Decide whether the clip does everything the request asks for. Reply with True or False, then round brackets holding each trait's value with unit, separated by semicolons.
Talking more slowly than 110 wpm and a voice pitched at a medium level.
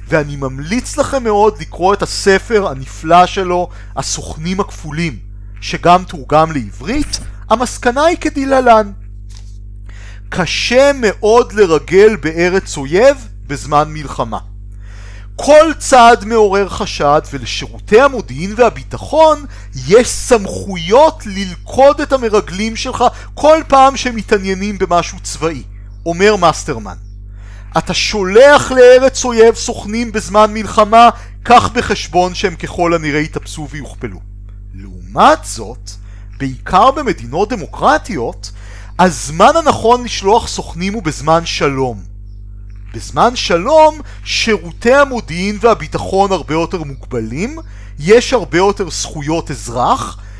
True (100 wpm; 175 Hz)